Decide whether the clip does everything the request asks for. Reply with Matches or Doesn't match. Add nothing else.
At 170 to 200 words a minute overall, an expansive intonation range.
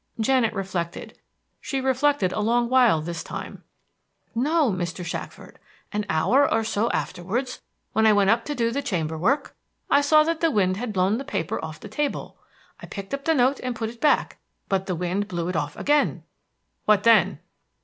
Matches